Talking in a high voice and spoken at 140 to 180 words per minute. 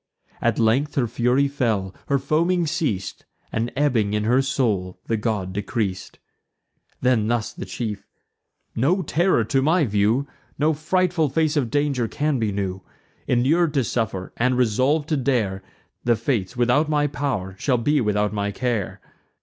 No: low, 125 Hz; average, 155 wpm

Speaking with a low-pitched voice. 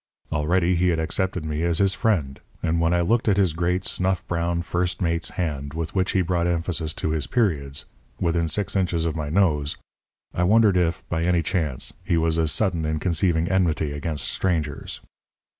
Yes: very low, 85 Hz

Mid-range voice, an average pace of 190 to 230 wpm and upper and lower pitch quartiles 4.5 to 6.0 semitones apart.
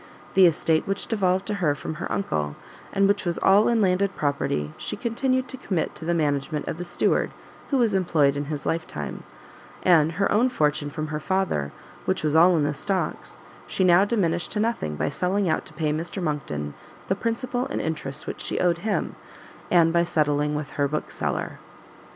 Yes: medium, 170 Hz; average, 195 wpm; average, 4.8 semitones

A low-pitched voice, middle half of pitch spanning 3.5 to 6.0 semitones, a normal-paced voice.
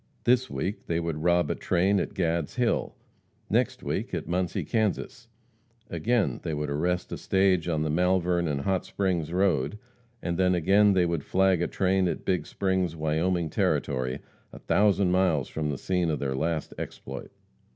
No: very low, 90 Hz; average, 3.0 semitones; average, 170 wpm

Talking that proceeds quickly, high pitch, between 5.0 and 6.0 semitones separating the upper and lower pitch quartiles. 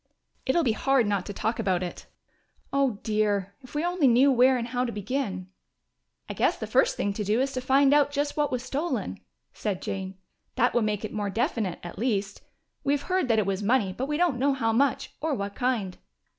Yes: fast, 220 wpm; high, 240 Hz; average, 5.3 semitones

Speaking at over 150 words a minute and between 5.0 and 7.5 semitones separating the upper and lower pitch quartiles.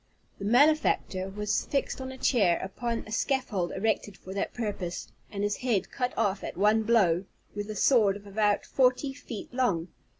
No: average, 175 wpm; average, 4.1 semitones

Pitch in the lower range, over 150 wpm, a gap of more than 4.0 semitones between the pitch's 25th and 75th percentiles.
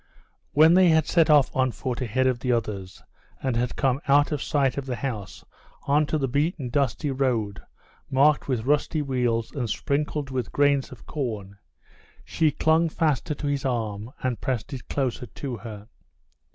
No: low, 130 Hz; average, 170 wpm; average, 3.5 semitones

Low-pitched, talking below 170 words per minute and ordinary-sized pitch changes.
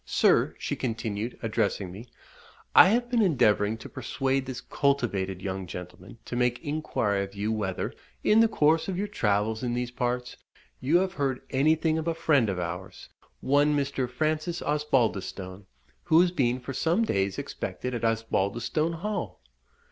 No: low, 125 Hz; average, 160 wpm; wide, 6.9 semitones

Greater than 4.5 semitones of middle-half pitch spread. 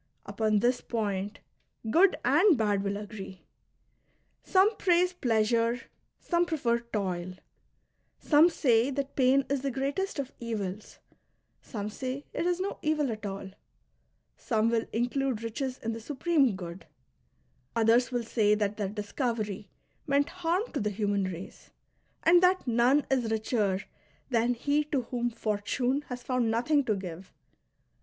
Yes: average, 4.9 semitones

